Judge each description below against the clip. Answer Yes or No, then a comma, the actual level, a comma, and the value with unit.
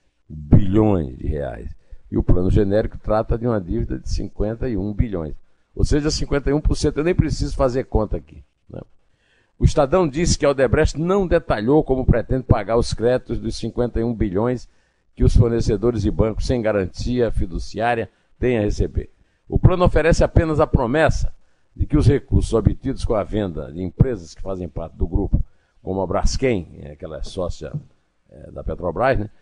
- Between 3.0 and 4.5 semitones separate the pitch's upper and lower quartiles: No, average, 5.2 semitones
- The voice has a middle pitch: No, low, 110 Hz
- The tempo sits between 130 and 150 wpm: No, average, 165 wpm